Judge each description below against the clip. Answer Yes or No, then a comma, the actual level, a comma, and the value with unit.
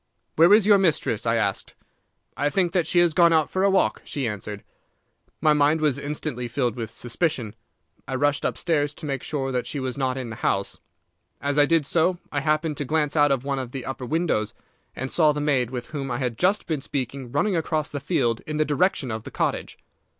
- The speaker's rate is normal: No, fast, 220 wpm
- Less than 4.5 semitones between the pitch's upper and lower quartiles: Yes, average, 3.9 semitones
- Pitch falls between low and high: Yes, medium, 145 Hz